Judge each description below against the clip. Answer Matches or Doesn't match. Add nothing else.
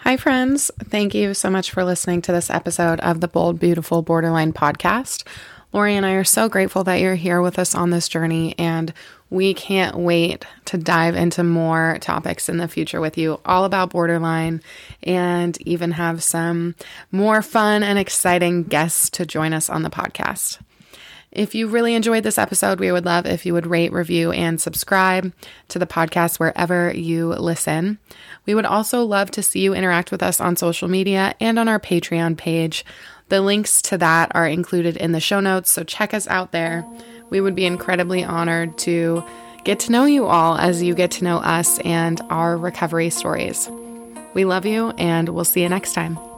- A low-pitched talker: Doesn't match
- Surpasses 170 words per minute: Matches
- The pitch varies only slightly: Matches